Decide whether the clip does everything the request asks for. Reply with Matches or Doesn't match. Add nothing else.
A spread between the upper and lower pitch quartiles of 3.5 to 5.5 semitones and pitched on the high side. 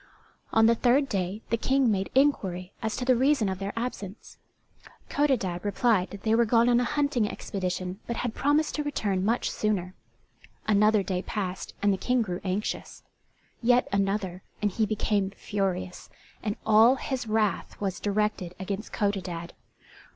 Matches